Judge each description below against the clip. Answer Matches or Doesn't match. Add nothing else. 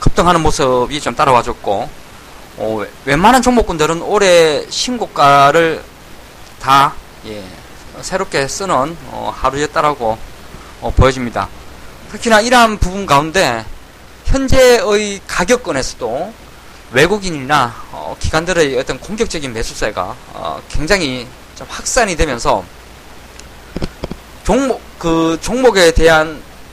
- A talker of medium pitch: Matches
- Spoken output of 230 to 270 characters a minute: Matches